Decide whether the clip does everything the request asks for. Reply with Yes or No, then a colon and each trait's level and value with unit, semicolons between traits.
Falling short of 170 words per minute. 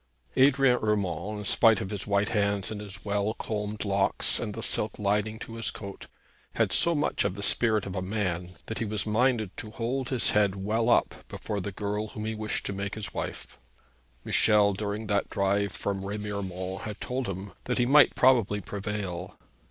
No: average, 190 wpm